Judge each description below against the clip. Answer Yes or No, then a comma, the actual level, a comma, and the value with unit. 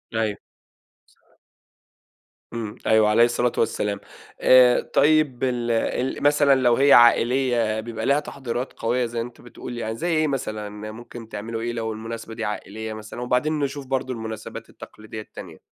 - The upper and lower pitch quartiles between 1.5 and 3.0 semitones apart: Yes, narrow, 2.6 semitones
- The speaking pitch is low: Yes, low, 120 Hz